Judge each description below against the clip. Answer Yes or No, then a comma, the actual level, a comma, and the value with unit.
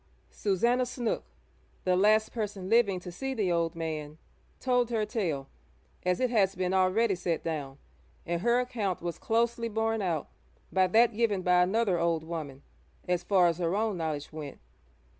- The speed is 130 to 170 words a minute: Yes, average, 165 wpm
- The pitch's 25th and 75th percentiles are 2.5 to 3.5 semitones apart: No, average, 4.8 semitones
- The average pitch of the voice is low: No, medium, 185 Hz